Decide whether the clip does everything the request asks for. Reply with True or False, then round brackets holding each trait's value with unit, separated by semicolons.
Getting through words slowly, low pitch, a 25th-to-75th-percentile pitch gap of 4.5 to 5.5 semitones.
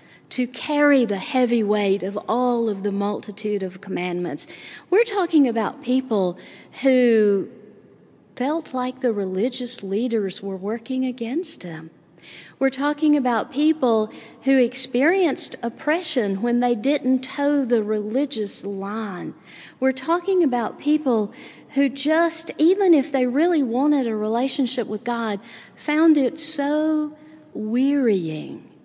False (125 wpm; 250 Hz; 5.2 semitones)